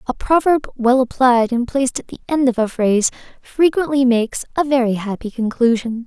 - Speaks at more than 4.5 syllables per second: Yes, 5.4 syllables/s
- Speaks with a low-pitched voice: No, very high, 250 Hz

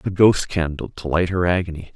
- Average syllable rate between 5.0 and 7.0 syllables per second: Yes, 5.3 syllables/s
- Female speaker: No, male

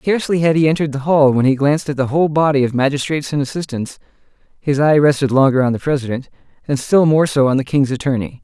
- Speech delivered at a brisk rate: Yes, fast, 230 wpm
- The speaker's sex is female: No, male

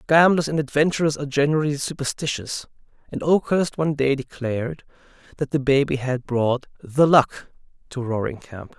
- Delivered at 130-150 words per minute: Yes, average, 145 wpm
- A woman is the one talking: No, male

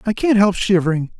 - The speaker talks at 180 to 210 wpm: Yes, average, 200 wpm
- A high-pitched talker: Yes, high, 195 Hz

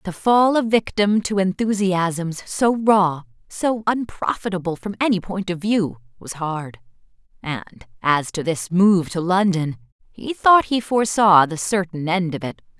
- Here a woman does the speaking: Yes, female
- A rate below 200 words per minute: Yes, average, 155 wpm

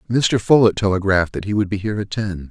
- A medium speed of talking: No, fast, 240 wpm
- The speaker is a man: Yes, male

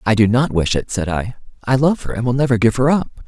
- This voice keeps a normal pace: No, fast, 295 wpm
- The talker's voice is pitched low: Yes, low, 120 Hz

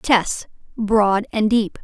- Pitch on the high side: Yes, high, 210 Hz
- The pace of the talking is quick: No, slow, 100 wpm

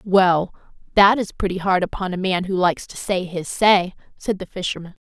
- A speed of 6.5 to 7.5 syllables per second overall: No, 5.2 syllables/s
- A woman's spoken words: Yes, female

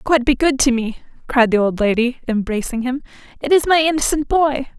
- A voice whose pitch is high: Yes, very high, 260 Hz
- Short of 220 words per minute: Yes, average, 200 wpm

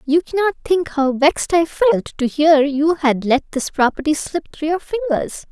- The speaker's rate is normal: Yes, average, 195 wpm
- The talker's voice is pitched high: Yes, very high, 300 Hz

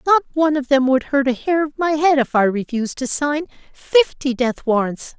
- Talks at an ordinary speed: No, fast, 220 wpm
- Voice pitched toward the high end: Yes, very high, 275 Hz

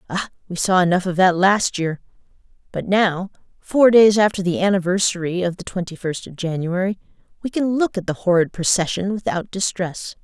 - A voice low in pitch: No, medium, 185 Hz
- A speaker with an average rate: Yes, average, 175 wpm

